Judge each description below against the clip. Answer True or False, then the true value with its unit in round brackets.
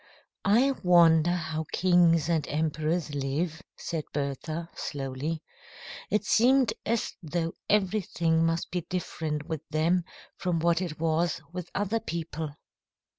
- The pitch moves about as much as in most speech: False (2.3 semitones)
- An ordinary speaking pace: False (125 wpm)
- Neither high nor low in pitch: True (165 Hz)